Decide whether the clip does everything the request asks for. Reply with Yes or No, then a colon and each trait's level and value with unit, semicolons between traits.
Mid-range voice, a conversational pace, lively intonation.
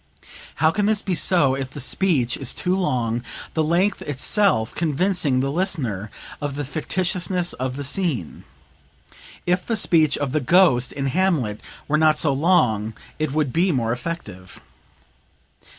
Yes: medium, 150 Hz; average, 150 wpm; wide, 5.7 semitones